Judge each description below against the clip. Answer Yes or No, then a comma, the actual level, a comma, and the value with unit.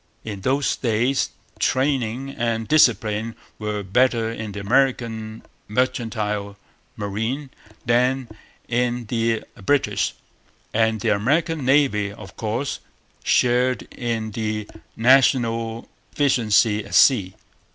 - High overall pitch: No, low, 115 Hz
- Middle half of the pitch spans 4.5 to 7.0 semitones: No, average, 3.2 semitones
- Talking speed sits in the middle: No, slow, 100 wpm